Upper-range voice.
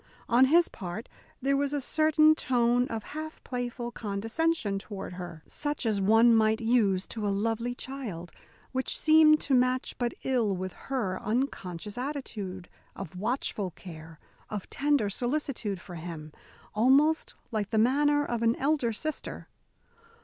Yes: high, 235 Hz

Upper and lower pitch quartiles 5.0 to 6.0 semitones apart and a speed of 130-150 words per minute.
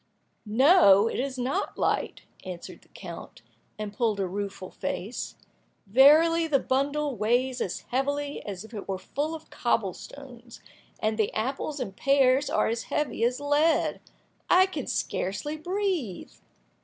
Yes: wide, 5.5 semitones; average, 145 wpm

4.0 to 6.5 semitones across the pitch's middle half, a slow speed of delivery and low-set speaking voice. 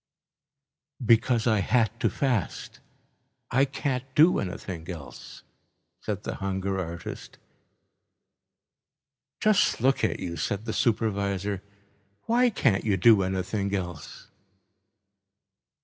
Yes: average, 4.4 semitones; slow, 100 wpm; low, 100 Hz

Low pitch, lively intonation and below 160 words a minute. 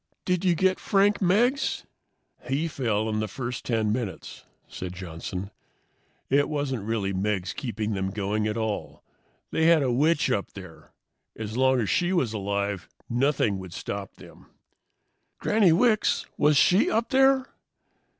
Yes: low, 120 Hz; wide, 8.5 semitones; average, 150 wpm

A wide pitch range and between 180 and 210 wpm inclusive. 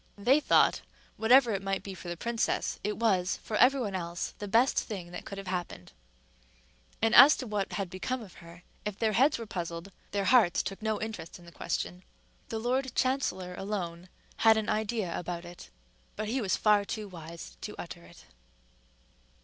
No: average, 4.1 semitones; average, 190 wpm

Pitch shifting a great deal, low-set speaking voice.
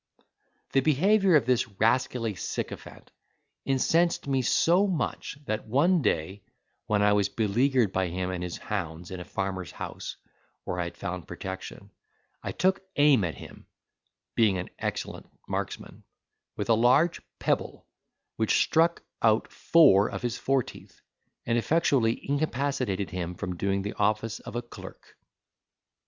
Yes: wide, 6.6 semitones; low, 115 Hz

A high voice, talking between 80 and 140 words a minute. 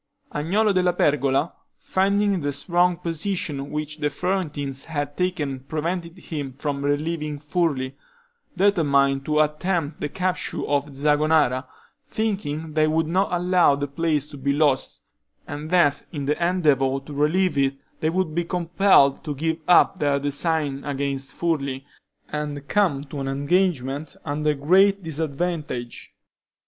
No: medium, 150 Hz; slow, 135 wpm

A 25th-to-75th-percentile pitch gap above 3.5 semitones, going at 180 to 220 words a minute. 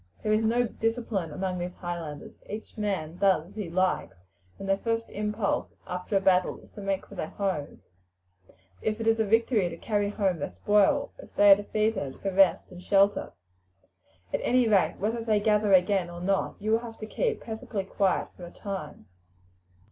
No: average, 3.0 semitones; average, 190 wpm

